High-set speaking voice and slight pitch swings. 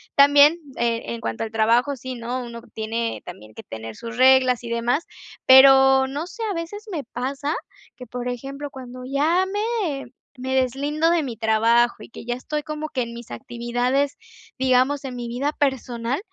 No: very high, 255 Hz; average, 3.3 semitones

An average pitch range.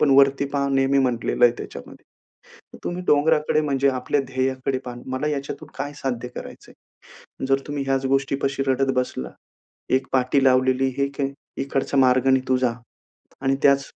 No: narrow, 1.1 semitones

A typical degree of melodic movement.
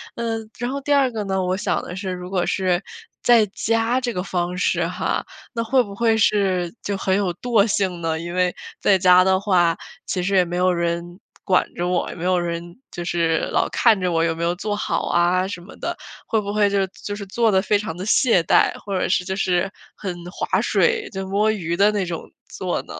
Yes: average, 3.1 semitones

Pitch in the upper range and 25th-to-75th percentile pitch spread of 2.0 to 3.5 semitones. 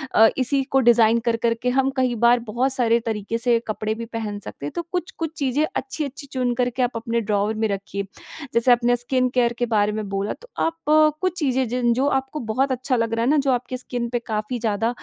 Yes: high, 245 Hz; narrow, 2.6 semitones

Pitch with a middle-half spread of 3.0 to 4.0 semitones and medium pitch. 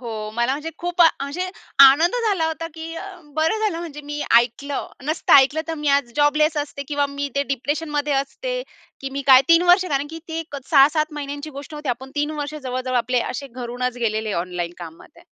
No: average, 3.6 semitones; very high, 285 Hz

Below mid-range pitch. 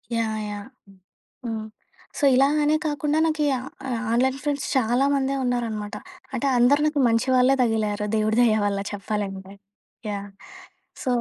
No: high, 235 Hz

